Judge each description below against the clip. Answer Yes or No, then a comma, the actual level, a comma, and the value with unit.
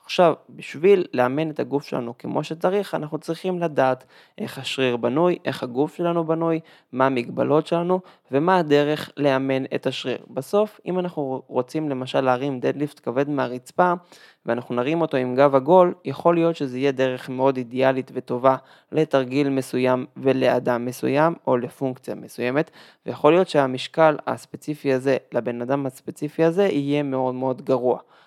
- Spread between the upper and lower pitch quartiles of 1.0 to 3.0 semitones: No, average, 3.7 semitones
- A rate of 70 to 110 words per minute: No, average, 145 wpm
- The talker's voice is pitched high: No, medium, 140 Hz